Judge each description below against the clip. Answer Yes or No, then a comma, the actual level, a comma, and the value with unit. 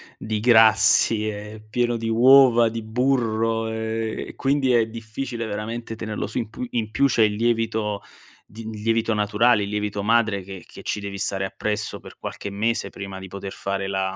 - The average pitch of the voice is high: No, low, 110 Hz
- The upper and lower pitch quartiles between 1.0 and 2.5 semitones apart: Yes, narrow, 1.8 semitones